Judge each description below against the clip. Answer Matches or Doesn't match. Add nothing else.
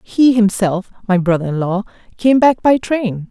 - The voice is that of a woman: Matches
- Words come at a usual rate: Matches